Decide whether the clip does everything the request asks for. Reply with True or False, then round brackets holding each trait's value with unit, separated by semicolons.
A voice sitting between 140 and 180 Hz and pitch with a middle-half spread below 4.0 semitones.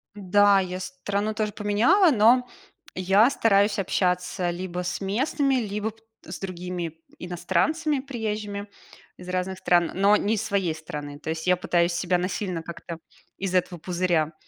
False (190 Hz; 2.9 semitones)